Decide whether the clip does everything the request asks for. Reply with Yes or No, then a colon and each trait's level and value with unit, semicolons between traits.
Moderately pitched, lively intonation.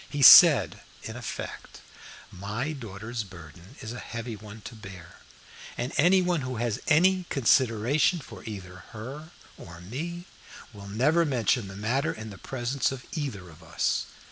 No: low, 115 Hz; wide, 5.8 semitones